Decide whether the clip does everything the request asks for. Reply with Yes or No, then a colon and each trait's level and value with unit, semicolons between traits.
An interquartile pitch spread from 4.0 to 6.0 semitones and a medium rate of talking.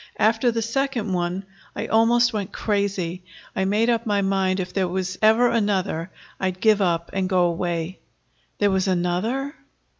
No: average, 3.3 semitones; average, 160 wpm